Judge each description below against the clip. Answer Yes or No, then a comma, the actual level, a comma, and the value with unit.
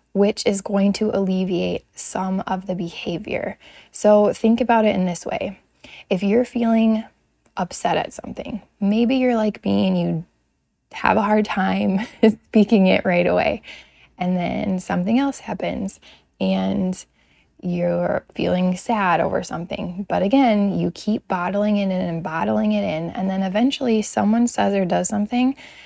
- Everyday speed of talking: Yes, average, 155 wpm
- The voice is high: Yes, high, 200 Hz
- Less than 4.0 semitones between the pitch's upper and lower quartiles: Yes, average, 3.3 semitones